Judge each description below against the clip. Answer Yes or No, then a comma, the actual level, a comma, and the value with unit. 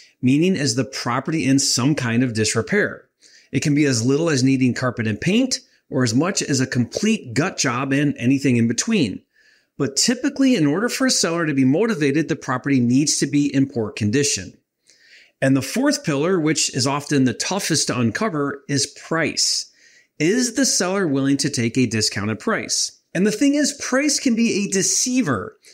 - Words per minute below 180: No, average, 185 wpm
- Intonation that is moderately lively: No, wide, 7.3 semitones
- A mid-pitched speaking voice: Yes, medium, 145 Hz